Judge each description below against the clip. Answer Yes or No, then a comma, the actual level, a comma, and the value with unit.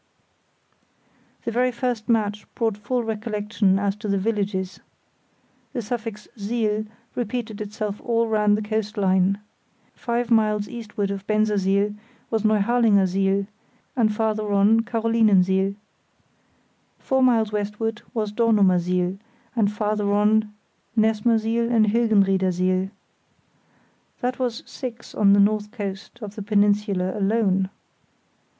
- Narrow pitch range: Yes, narrow, 2.2 semitones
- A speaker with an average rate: No, slow, 115 wpm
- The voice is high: Yes, high, 210 Hz